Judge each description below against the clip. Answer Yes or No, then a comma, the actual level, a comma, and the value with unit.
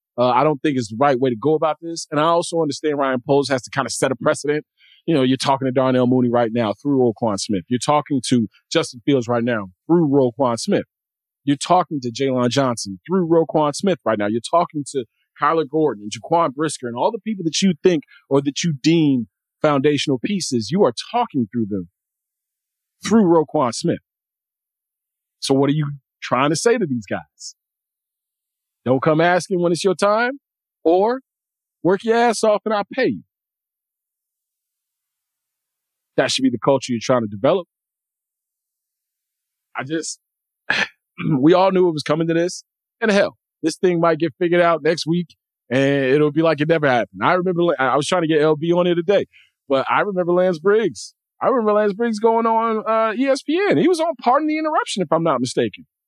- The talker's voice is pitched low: No, medium, 155 Hz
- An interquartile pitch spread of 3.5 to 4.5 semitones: No, wide, 5.6 semitones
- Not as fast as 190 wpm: No, average, 195 wpm